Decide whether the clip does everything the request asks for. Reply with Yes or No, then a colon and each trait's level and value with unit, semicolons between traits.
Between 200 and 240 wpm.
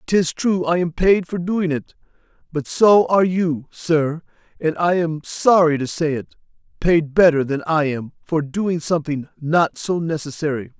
No: average, 170 wpm